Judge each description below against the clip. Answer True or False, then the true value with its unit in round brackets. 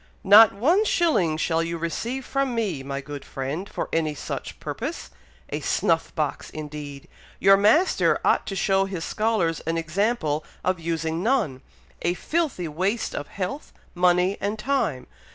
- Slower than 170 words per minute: True (150 wpm)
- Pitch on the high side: False (180 Hz)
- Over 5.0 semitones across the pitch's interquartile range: True (5.6 semitones)